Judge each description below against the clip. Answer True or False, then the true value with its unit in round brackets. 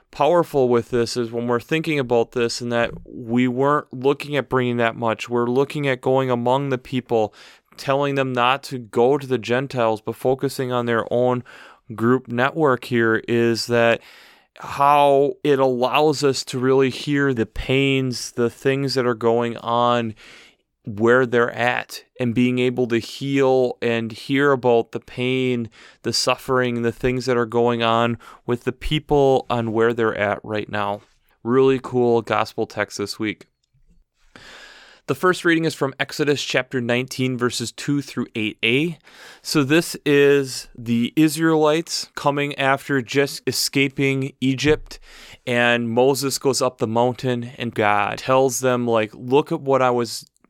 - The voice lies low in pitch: True (125 Hz)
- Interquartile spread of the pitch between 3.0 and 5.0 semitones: False (2.6 semitones)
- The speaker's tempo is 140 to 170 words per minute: True (155 wpm)